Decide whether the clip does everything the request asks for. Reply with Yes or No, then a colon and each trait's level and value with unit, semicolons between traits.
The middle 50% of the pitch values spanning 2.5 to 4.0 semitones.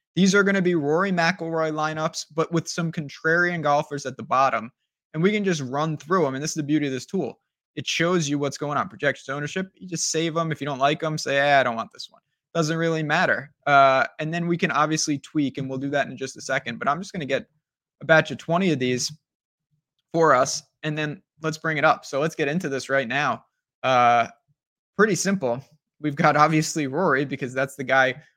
Yes: average, 2.9 semitones